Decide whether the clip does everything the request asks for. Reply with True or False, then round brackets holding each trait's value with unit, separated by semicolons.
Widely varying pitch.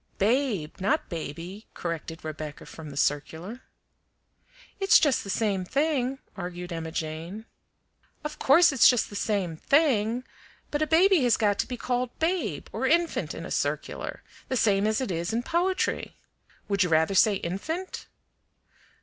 True (8.2 semitones)